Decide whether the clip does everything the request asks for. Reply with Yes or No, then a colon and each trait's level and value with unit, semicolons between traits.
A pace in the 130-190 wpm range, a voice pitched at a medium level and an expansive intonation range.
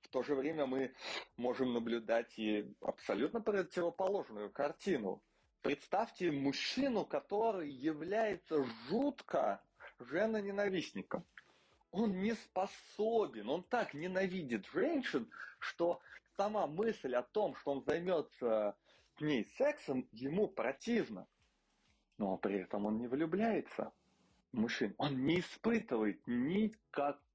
No: slow, 110 wpm; medium, 175 Hz; wide, 8.1 semitones